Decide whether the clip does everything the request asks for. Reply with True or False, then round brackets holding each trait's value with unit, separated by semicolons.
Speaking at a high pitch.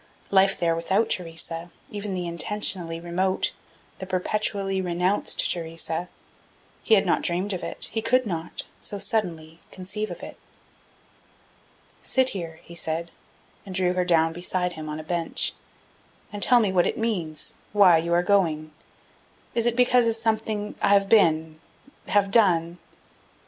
False (180 Hz)